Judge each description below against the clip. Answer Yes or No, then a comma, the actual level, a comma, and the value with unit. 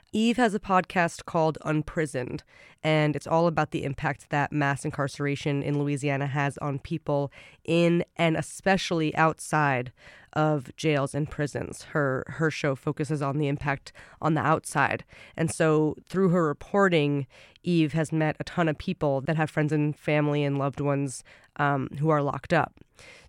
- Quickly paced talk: No, average, 160 wpm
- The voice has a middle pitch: Yes, medium, 150 Hz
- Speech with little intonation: Yes, narrow, 2.1 semitones